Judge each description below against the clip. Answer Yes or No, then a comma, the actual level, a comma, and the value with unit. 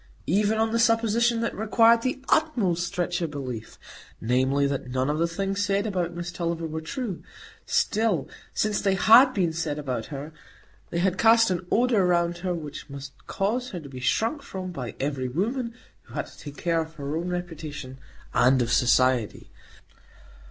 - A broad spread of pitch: Yes, wide, 6.8 semitones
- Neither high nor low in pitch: Yes, medium, 175 Hz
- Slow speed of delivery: No, average, 170 wpm